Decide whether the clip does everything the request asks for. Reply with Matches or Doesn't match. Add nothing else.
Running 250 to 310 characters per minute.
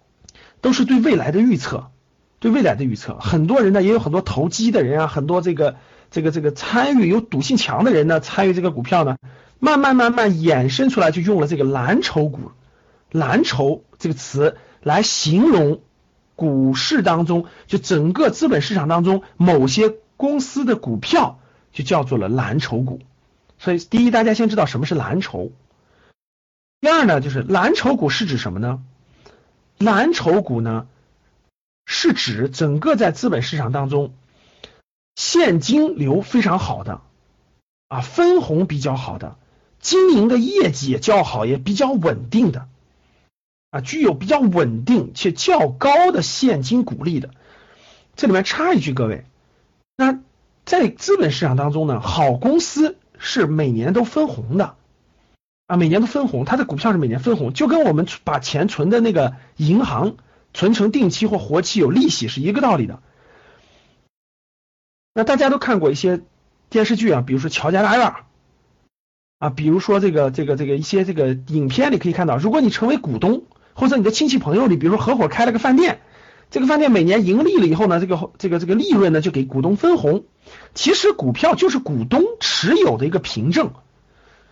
Matches